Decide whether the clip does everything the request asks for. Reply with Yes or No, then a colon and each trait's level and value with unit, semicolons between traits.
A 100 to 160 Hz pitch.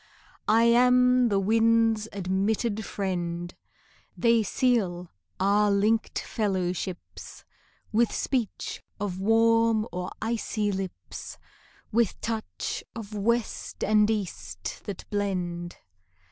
No: high, 210 Hz